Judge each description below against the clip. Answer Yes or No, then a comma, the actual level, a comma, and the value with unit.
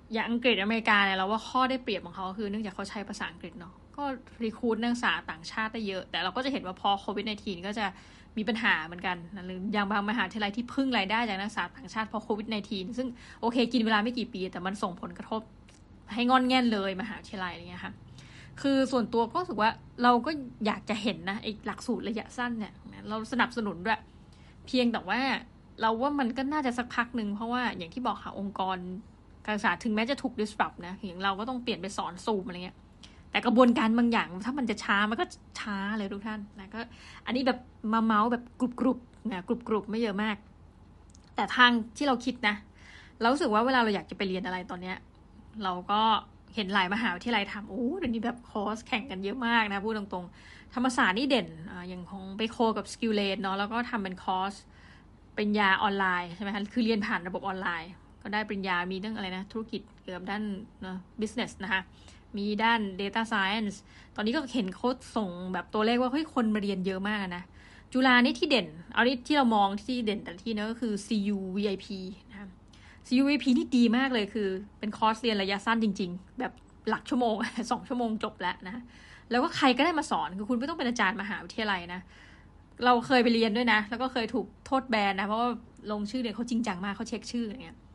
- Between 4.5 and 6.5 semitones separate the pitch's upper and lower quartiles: No, average, 3.4 semitones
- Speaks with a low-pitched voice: No, high, 215 Hz